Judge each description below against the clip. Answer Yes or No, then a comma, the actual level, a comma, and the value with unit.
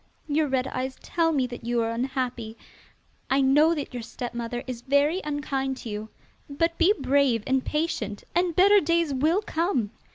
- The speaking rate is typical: Yes, average, 170 wpm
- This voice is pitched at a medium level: No, very high, 270 Hz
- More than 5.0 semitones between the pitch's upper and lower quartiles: No, average, 4.6 semitones